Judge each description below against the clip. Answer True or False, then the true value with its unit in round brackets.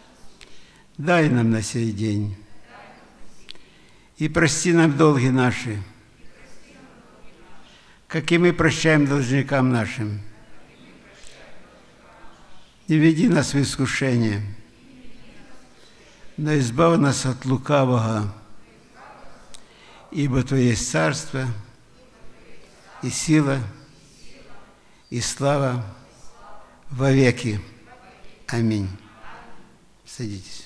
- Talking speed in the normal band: False (75 wpm)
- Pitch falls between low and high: False (130 Hz)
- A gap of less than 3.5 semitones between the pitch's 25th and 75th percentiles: False (5.5 semitones)